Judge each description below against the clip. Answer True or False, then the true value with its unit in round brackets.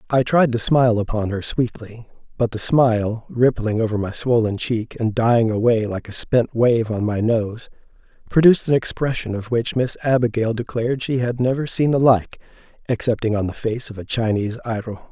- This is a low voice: True (115 Hz)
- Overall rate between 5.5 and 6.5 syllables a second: False (5.2 syllables/s)